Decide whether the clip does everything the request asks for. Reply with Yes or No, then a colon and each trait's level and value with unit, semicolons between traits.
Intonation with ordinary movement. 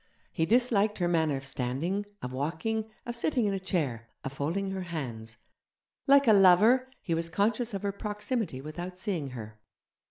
No: wide, 6.8 semitones